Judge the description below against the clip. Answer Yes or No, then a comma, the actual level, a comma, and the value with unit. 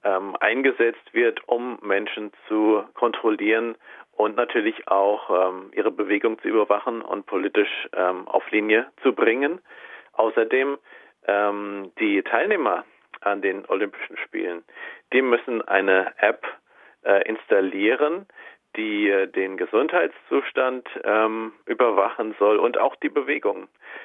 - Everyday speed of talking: No, slow, 115 wpm